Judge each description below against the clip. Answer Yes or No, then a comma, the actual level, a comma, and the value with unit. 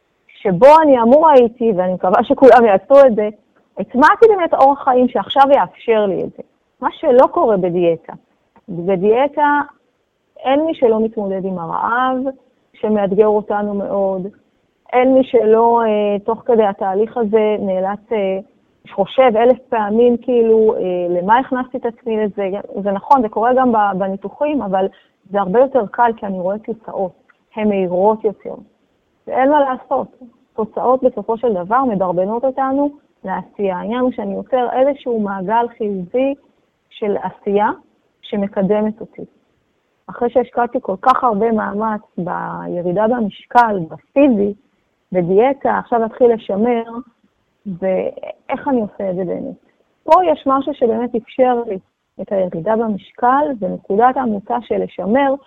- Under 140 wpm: Yes, average, 130 wpm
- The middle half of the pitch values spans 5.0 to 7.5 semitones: No, average, 4.3 semitones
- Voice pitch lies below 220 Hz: No, high, 230 Hz